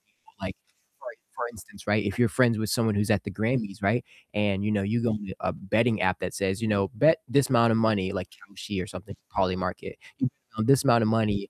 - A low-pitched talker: Yes, low, 105 Hz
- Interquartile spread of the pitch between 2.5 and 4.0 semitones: Yes, average, 2.9 semitones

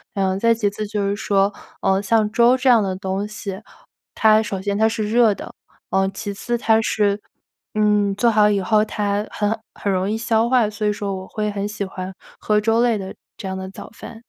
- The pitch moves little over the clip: Yes, narrow, 1.9 semitones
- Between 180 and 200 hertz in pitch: No, high, 210 Hz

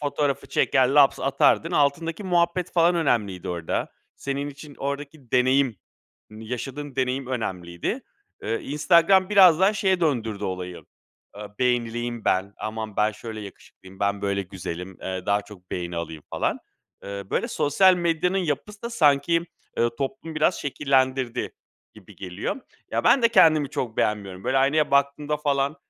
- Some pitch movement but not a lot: No, wide, 6.7 semitones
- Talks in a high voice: No, low, 135 Hz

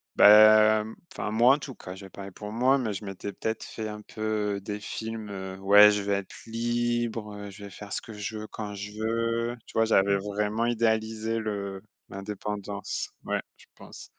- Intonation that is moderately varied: No, narrow, 1.8 semitones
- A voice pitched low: Yes, low, 105 Hz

